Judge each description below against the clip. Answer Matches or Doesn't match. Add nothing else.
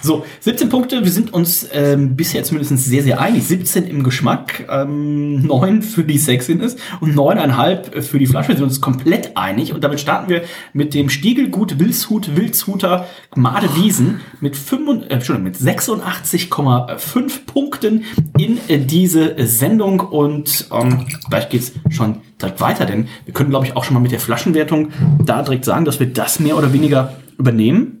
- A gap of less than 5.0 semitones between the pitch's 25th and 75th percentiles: Doesn't match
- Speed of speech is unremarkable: Matches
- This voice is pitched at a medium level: Matches